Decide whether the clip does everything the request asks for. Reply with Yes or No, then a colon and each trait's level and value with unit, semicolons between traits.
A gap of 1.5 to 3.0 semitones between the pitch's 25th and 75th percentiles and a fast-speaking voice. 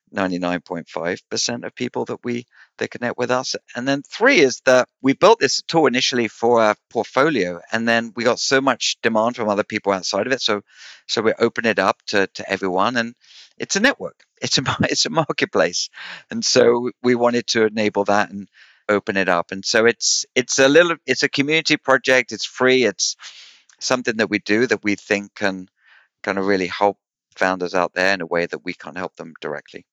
No: average, 4.4 semitones; fast, 210 wpm